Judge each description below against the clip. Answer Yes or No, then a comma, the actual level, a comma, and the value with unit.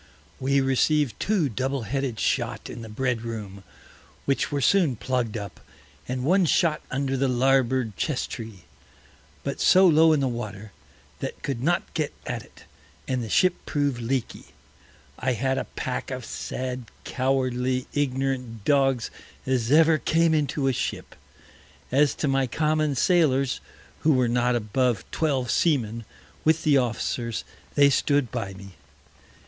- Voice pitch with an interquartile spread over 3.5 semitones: No, average, 3.1 semitones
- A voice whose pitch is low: Yes, low, 130 Hz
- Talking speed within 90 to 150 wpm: Yes, average, 145 wpm